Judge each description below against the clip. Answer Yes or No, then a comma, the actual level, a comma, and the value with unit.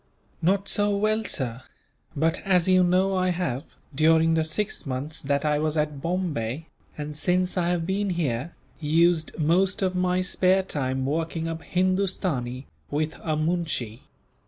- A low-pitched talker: No, medium, 165 Hz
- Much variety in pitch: No, average, 3.7 semitones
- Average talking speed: Yes, average, 155 wpm